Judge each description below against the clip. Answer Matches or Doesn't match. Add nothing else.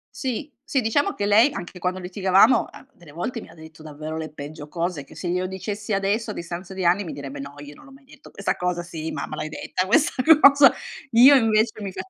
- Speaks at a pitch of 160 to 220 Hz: Matches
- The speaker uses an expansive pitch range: Matches